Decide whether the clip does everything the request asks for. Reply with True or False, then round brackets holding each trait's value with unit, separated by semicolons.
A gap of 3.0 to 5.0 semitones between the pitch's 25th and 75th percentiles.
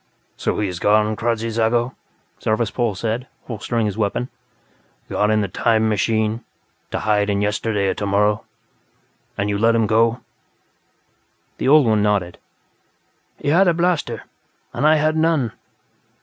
False (2.5 semitones)